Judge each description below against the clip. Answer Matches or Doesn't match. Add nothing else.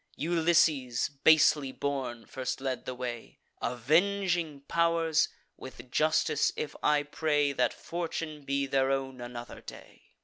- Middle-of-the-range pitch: Matches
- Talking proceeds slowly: Matches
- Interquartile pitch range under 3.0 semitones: Doesn't match